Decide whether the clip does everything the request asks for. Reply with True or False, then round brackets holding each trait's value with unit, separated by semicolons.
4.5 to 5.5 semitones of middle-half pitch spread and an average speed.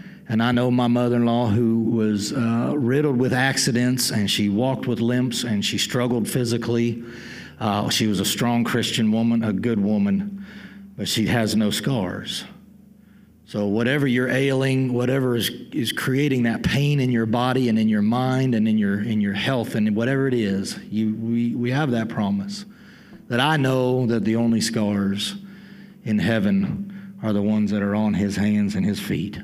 False (3.8 semitones; 185 wpm)